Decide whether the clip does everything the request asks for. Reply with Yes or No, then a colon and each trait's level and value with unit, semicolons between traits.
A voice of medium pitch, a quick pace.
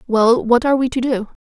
No: high, 240 Hz; fast, 250 wpm